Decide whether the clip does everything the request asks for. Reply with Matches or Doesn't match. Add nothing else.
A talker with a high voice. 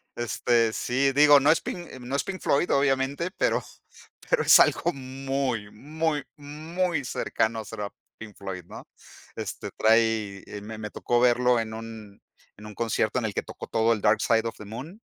Doesn't match